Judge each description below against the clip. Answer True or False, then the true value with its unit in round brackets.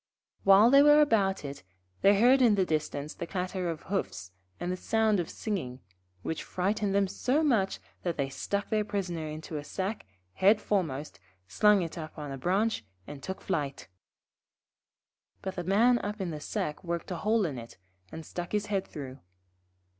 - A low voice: False (190 Hz)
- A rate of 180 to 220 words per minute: True (185 wpm)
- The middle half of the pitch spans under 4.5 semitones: False (5.1 semitones)